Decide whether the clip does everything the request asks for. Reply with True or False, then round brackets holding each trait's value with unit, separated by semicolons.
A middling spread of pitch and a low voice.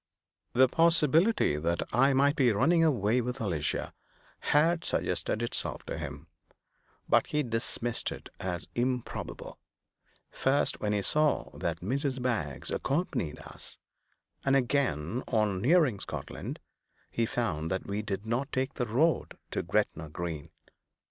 False (6.1 semitones; 120 Hz)